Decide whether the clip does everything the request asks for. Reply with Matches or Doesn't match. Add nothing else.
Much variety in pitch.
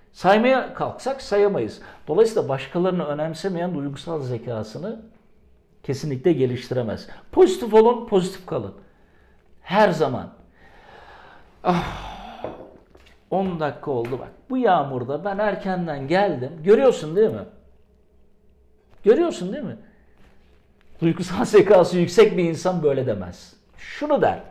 Matches